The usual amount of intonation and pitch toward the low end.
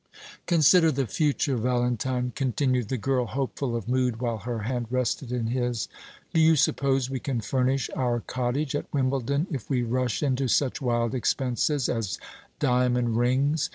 No: narrow, 2.1 semitones; low, 125 Hz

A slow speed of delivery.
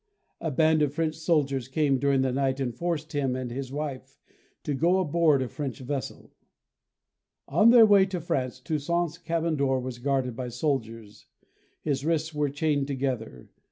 No: average, 165 wpm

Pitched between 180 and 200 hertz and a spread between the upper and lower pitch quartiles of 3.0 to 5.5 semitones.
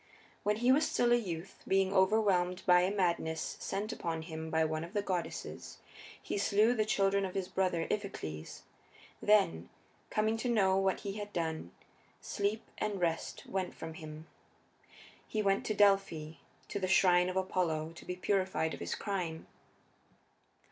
Yes: high, 190 Hz; average, 3.6 semitones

